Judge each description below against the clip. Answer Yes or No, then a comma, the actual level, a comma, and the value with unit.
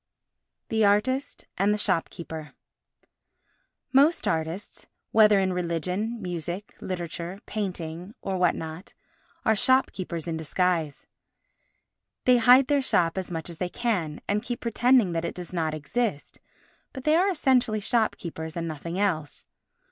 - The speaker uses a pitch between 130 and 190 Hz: Yes, medium, 185 Hz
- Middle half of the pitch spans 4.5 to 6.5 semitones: Yes, average, 5.1 semitones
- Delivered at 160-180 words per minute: No, slow, 135 wpm